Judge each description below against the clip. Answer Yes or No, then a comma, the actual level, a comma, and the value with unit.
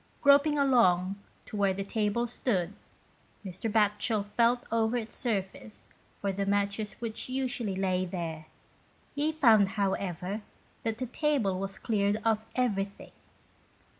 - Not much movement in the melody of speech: No, average, 3.4 semitones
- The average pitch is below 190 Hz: No, high, 210 Hz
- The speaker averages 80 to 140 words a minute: Yes, slow, 135 wpm